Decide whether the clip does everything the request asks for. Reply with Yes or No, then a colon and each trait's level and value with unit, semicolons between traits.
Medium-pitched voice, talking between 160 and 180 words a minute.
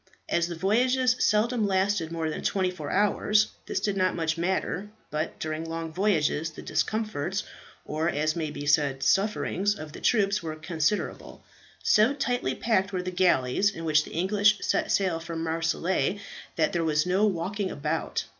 Yes: medium, 180 Hz; average, 170 wpm